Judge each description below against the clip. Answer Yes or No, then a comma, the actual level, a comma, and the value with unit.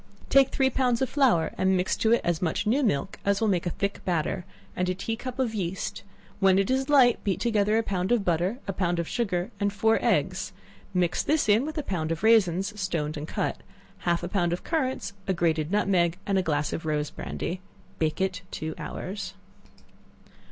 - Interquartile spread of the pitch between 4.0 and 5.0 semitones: Yes, average, 4.5 semitones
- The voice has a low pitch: No, high, 190 Hz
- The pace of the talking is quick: Yes, fast, 210 wpm